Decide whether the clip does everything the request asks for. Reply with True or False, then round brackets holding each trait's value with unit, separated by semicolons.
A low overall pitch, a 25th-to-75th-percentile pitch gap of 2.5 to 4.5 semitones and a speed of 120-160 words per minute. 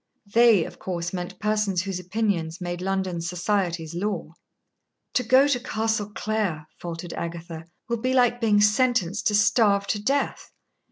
False (200 Hz; 4.0 semitones; 150 wpm)